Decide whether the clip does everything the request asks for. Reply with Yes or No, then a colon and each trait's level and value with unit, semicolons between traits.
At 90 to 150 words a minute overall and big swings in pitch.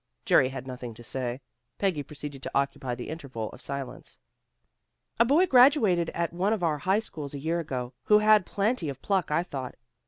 No: average, 190 wpm; wide, 6.9 semitones